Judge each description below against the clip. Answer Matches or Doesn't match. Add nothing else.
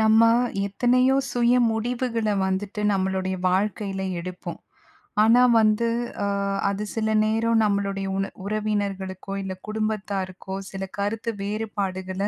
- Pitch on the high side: Matches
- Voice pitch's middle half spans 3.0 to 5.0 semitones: Doesn't match